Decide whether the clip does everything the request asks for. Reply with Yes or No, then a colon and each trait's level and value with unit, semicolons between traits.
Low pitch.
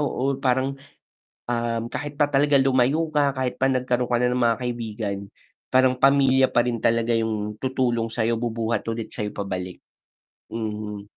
Yes: low, 120 Hz